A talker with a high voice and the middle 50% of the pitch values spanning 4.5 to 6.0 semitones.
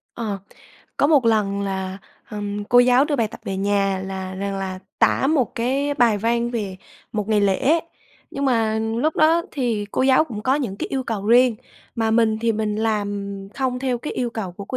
No: high, 225 Hz; average, 3.9 semitones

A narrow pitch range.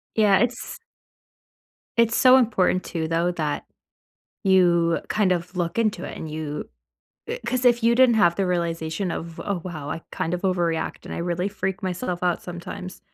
No: average, 3.3 semitones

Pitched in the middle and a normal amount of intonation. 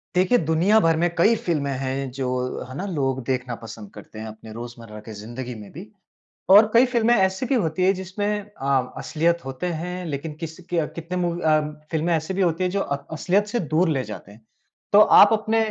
No: medium, 160 Hz; wide, 6.0 semitones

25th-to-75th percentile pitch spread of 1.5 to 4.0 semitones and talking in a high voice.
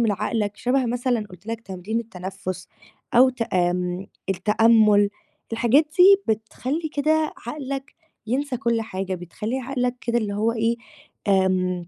No: average, 4.5 semitones; high, 225 Hz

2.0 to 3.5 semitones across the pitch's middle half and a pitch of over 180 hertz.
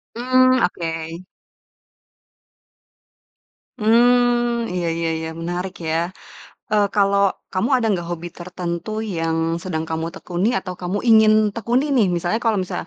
No: average, 5.1 semitones; high, 190 Hz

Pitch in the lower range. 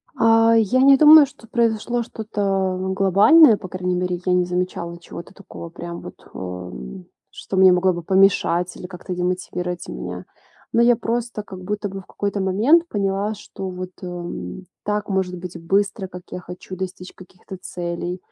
No: high, 190 Hz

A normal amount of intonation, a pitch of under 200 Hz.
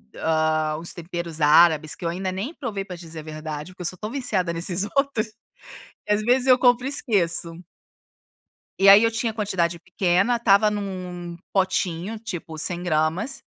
Yes: average, 4.4 semitones; medium, 185 Hz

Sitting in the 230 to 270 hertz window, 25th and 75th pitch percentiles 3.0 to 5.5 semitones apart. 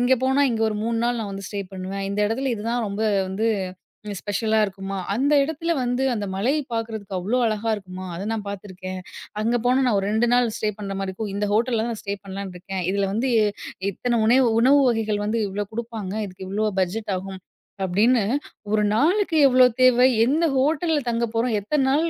No: high, 220 Hz; average, 3.8 semitones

